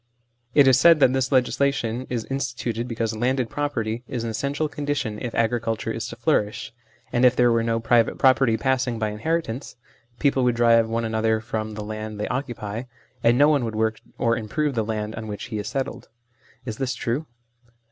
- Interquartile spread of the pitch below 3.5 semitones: Yes, average, 2.9 semitones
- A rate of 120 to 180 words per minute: No, average, 190 wpm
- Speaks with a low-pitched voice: Yes, low, 115 Hz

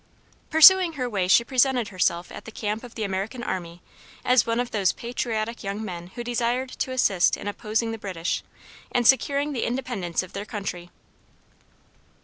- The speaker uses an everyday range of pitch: Yes, average, 4.1 semitones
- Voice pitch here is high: Yes, high, 225 Hz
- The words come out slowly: No, average, 170 wpm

